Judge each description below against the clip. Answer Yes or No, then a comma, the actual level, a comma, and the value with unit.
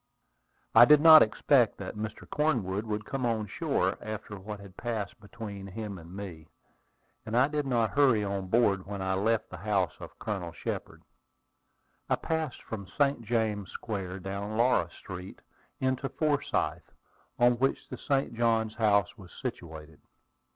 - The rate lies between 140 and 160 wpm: Yes, average, 155 wpm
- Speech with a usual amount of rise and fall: Yes, average, 3.7 semitones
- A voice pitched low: Yes, low, 110 Hz